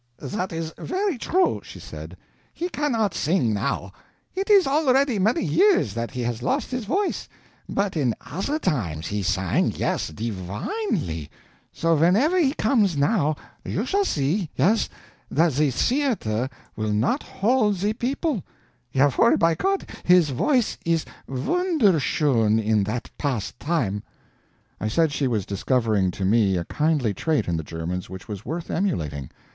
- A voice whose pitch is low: No, medium, 155 Hz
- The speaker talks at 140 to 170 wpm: Yes, average, 150 wpm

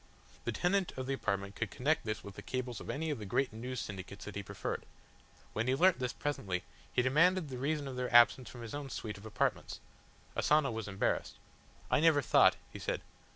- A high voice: No, low, 125 Hz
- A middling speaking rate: No, fast, 210 wpm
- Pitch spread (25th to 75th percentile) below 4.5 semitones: No, average, 5.1 semitones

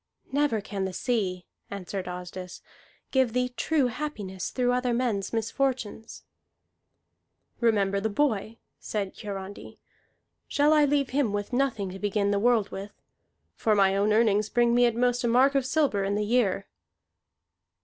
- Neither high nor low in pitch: No, high, 220 Hz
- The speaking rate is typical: Yes, average, 150 wpm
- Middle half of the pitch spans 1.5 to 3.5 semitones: No, average, 4.0 semitones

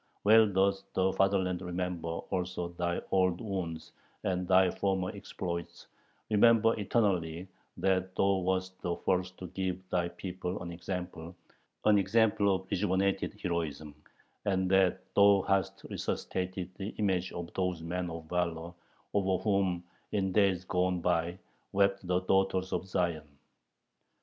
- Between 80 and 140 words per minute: Yes, slow, 135 wpm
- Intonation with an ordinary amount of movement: No, narrow, 1.6 semitones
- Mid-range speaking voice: No, very low, 95 Hz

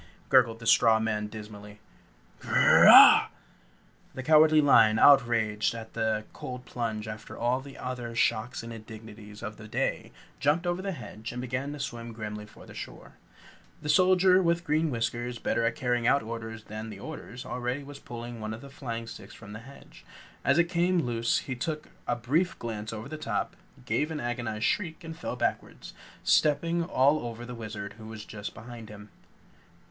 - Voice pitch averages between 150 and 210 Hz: No, low, 120 Hz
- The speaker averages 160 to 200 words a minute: Yes, average, 180 wpm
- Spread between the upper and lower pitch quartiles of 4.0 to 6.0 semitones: Yes, average, 4.4 semitones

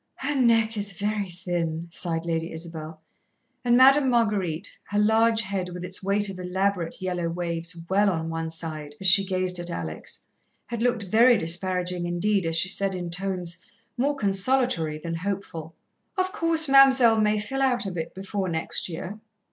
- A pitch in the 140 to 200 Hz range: Yes, high, 190 Hz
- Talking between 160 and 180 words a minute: Yes, average, 170 wpm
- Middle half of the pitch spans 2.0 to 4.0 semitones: No, average, 4.5 semitones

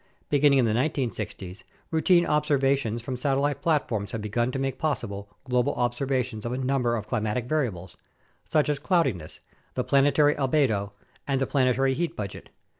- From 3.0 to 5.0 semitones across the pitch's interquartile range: Yes, average, 4.1 semitones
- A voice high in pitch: No, low, 130 Hz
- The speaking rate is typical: Yes, average, 160 wpm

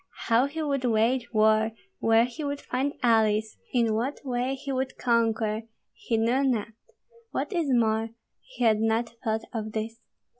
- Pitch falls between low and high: No, high, 230 Hz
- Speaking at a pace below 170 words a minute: Yes, average, 160 wpm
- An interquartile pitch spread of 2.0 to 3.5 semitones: Yes, average, 3.0 semitones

